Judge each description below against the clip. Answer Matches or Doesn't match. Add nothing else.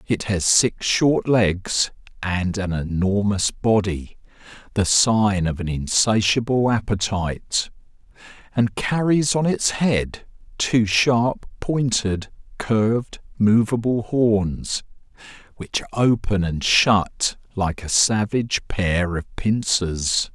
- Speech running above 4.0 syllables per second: Doesn't match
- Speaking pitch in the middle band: Doesn't match